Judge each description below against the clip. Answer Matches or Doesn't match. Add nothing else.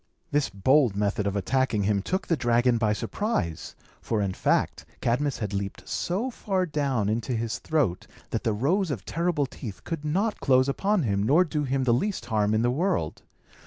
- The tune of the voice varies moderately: Doesn't match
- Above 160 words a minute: Matches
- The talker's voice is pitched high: Doesn't match